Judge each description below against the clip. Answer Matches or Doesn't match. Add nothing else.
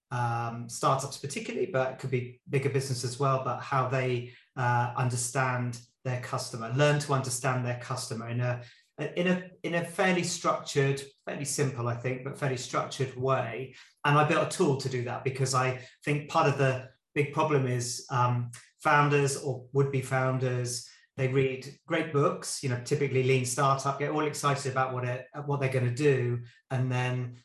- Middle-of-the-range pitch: Doesn't match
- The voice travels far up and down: Doesn't match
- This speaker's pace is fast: Doesn't match